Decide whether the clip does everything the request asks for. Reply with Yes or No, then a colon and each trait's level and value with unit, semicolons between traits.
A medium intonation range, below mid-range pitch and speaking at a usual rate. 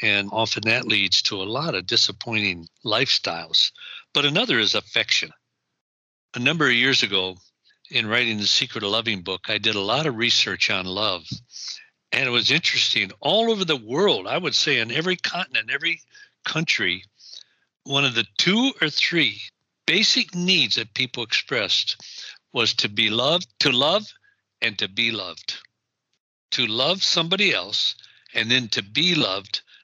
No: wide, 7.0 semitones; low, 120 Hz; average, 160 wpm